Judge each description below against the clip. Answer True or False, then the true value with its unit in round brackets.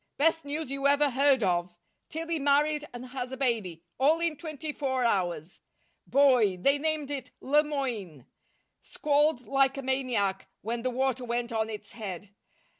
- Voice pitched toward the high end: True (265 Hz)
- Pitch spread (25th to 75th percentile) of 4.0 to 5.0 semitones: True (4.3 semitones)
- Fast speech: False (160 wpm)